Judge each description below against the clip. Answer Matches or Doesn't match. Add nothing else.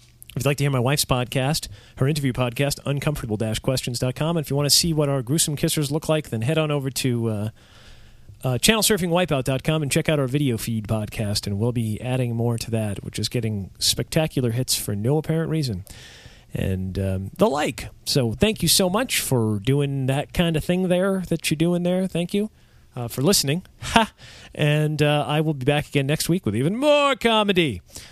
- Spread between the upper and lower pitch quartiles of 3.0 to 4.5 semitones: Doesn't match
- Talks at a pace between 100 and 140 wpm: Doesn't match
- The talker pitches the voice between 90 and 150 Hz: Matches